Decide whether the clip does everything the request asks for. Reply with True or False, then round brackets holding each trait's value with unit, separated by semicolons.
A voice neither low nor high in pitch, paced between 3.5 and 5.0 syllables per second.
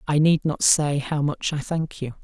True (150 Hz; 4.4 syllables/s)